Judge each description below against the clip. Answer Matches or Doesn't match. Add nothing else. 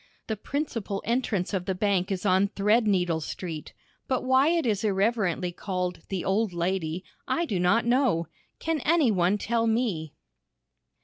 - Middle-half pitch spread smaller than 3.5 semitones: Doesn't match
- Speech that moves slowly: Doesn't match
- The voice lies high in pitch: Matches